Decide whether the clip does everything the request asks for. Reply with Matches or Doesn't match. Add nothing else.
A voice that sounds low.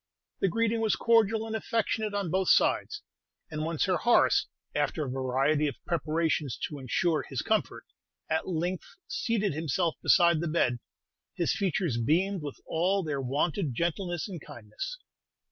Doesn't match